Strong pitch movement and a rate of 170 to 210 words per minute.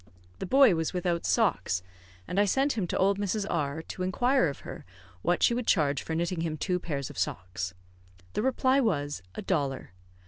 Yes: wide, 6.3 semitones; average, 195 wpm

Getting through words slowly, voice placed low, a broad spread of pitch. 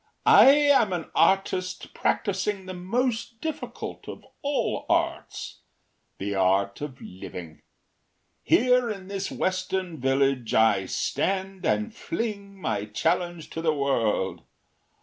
No: slow, 115 wpm; medium, 185 Hz; wide, 8.4 semitones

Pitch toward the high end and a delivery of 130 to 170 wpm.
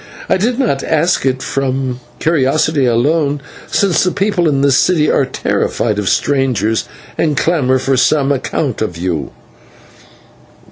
No: medium, 140 Hz; average, 140 wpm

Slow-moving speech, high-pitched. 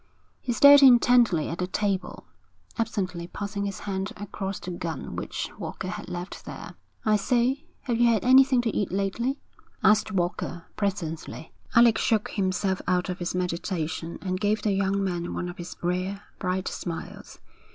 No: average, 160 wpm; high, 195 Hz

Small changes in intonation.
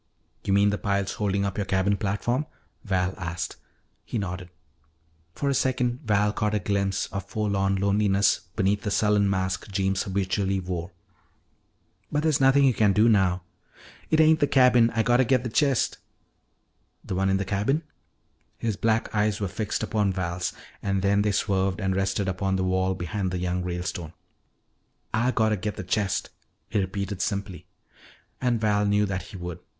Yes: narrow, 2.3 semitones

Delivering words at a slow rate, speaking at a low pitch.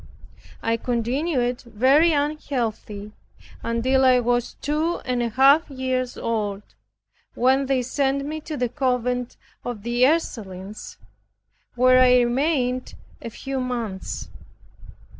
No: slow, 115 wpm; very high, 250 Hz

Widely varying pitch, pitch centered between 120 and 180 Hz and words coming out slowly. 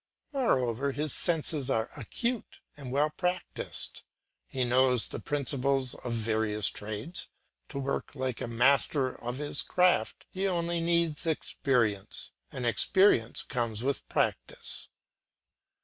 No: average, 5.0 semitones; low, 135 Hz; slow, 125 wpm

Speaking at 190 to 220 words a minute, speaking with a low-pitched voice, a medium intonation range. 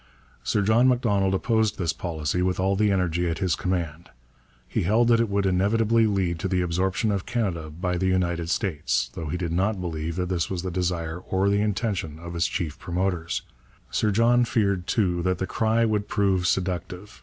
Yes: average, 195 wpm; very low, 95 Hz; average, 3.1 semitones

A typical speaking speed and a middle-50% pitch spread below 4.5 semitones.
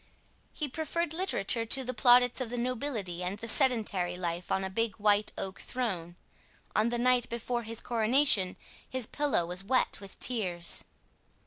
No: average, 160 wpm; average, 4.8 semitones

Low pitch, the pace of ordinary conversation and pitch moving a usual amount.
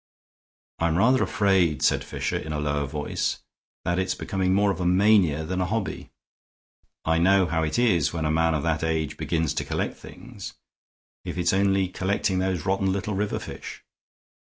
Yes: very low, 90 Hz; average, 180 wpm; average, 3.3 semitones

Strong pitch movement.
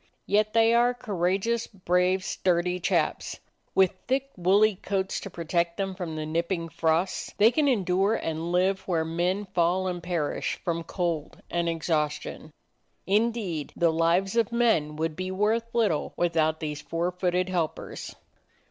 No: average, 3.2 semitones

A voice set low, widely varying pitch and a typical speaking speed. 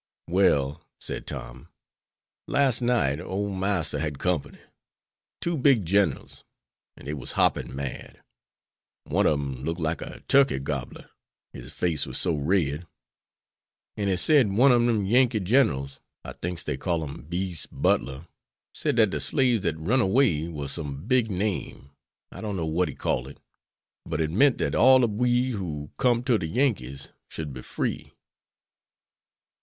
Yes: very low, 90 Hz; wide, 8.0 semitones; average, 160 wpm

